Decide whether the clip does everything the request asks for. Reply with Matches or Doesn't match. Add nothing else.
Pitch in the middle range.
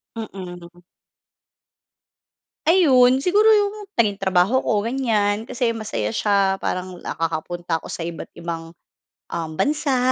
Doesn't match